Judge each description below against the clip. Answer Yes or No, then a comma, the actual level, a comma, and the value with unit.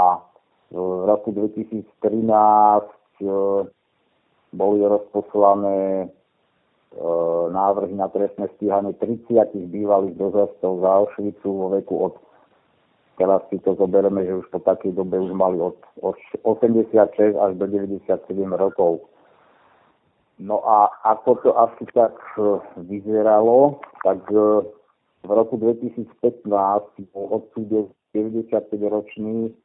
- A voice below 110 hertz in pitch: Yes, low, 100 Hz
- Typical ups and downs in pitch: No, narrow, 1.8 semitones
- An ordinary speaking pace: No, slow, 105 wpm